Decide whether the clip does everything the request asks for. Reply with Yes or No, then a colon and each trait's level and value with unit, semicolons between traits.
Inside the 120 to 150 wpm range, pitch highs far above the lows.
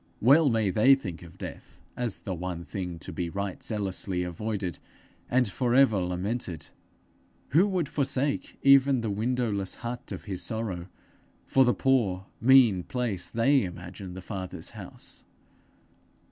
Yes: average, 145 wpm; wide, 5.7 semitones